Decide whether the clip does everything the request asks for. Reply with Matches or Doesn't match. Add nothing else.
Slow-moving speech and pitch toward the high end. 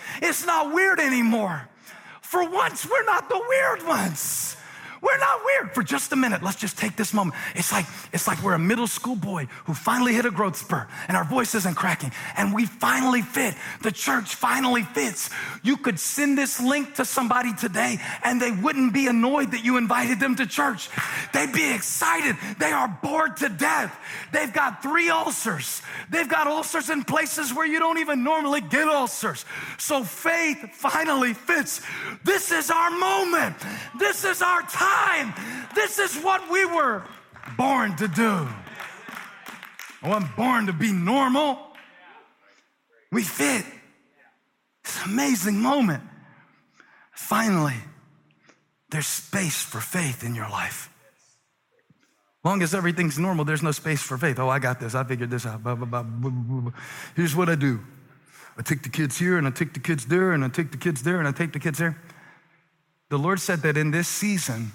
Doesn't match